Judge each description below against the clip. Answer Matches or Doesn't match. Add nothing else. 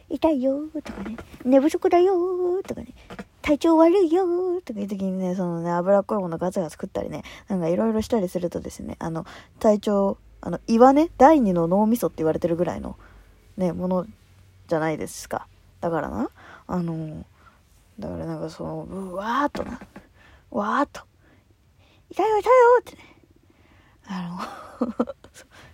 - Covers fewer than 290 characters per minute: Doesn't match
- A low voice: Doesn't match